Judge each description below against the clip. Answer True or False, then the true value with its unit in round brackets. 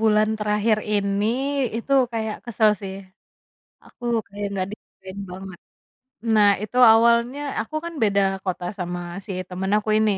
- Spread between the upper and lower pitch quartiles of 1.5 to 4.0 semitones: True (2.4 semitones)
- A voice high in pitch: True (210 Hz)